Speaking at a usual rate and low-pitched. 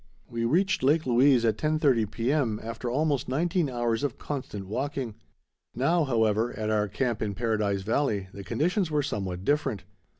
Yes: average, 160 wpm; low, 120 Hz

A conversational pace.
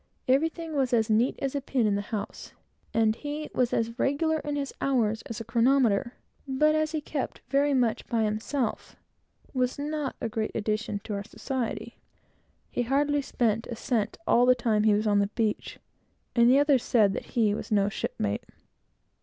Yes: average, 180 wpm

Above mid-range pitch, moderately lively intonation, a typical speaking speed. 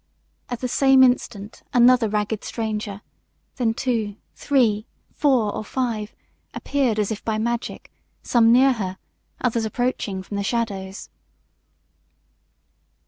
No: high, 225 Hz; average, 3.0 semitones; slow, 120 wpm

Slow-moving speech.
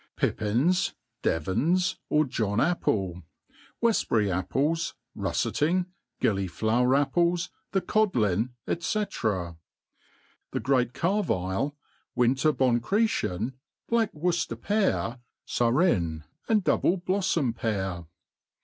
Yes: slow, 80 wpm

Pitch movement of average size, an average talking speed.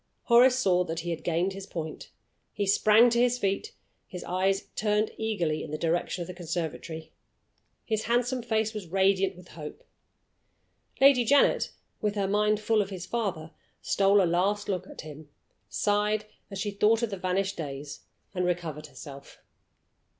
Yes: average, 3.9 semitones; average, 165 wpm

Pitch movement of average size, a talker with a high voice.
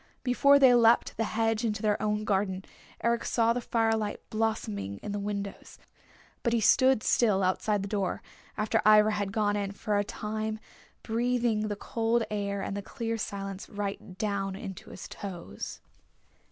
No: narrow, 2.1 semitones; high, 210 Hz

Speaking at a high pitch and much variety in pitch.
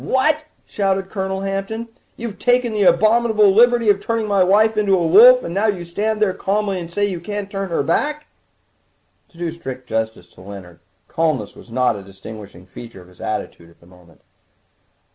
Yes: high, 195 Hz; wide, 8.9 semitones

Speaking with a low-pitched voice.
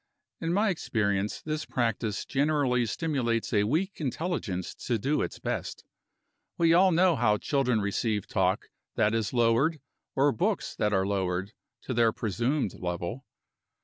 Yes: low, 120 Hz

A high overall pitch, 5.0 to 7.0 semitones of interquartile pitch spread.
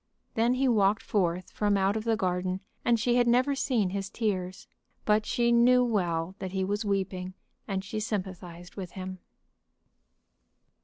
No: high, 200 Hz; average, 3.6 semitones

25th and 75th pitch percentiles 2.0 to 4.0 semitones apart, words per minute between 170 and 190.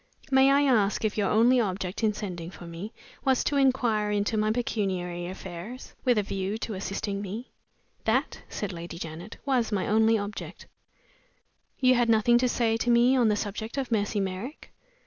Yes: average, 3.7 semitones; average, 180 wpm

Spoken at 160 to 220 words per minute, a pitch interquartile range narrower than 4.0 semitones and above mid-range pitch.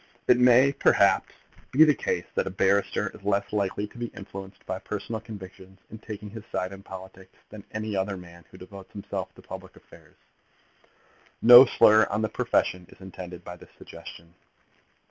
No: average, 175 wpm; narrow, 2.6 semitones; low, 100 Hz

